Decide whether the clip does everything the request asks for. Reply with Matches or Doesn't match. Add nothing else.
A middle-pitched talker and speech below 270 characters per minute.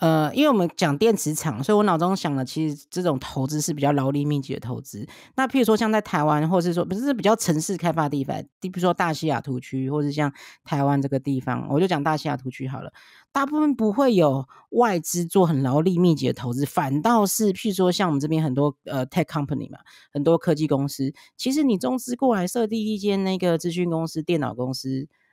Doesn't match